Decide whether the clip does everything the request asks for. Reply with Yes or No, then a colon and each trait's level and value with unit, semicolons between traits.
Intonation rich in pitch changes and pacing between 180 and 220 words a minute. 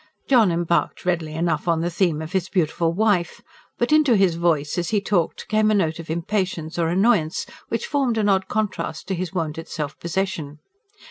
No: average, 3.8 semitones; average, 190 wpm